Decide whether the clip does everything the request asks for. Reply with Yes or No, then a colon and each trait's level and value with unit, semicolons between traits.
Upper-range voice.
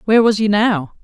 Yes: high, 210 Hz